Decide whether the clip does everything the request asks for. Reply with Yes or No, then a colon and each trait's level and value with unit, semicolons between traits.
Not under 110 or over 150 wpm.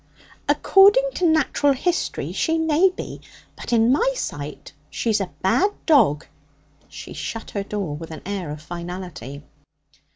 Yes: average, 140 wpm